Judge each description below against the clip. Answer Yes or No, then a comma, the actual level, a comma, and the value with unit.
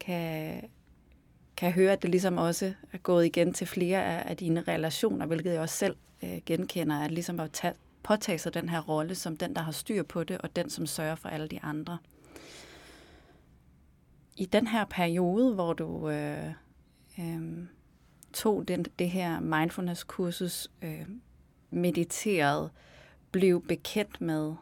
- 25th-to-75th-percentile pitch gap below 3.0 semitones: Yes, narrow, 2.4 semitones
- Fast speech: No, average, 150 wpm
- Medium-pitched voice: Yes, medium, 170 Hz